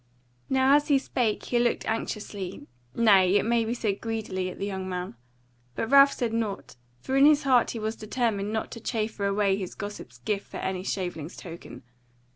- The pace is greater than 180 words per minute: Yes, average, 190 wpm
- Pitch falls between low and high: No, high, 215 Hz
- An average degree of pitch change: Yes, average, 3.5 semitones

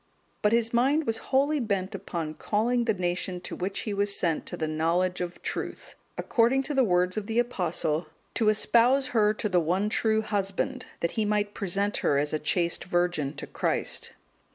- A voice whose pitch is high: Yes, high, 200 Hz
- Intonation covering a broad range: No, average, 4.5 semitones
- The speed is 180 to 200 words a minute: Yes, average, 190 wpm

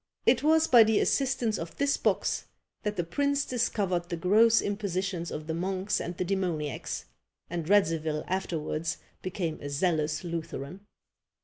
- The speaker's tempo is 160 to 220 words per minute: No, average, 145 wpm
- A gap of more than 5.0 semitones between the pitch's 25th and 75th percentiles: No, average, 4.2 semitones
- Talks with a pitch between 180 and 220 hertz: Yes, medium, 185 Hz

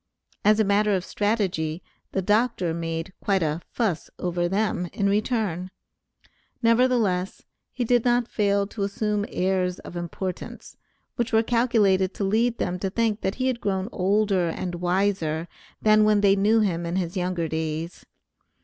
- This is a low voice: No, high, 195 Hz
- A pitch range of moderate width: Yes, average, 3.2 semitones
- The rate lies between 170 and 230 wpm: No, average, 160 wpm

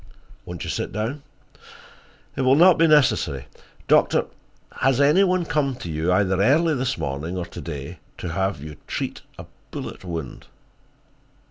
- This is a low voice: Yes, low, 105 Hz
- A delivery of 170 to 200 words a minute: No, average, 155 wpm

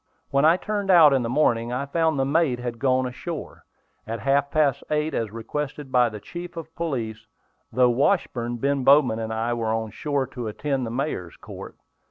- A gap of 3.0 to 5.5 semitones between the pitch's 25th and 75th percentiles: Yes, average, 4.3 semitones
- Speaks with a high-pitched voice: No, low, 135 Hz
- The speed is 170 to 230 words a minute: Yes, average, 195 wpm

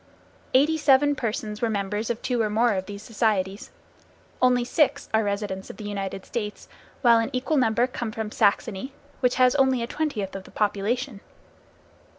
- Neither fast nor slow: Yes, average, 170 wpm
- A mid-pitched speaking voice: No, high, 225 Hz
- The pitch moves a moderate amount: Yes, average, 3.6 semitones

